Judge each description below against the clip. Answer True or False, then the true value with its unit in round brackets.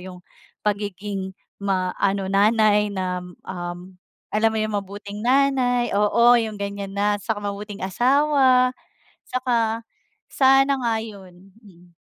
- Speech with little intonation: False (3.5 semitones)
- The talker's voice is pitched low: False (205 Hz)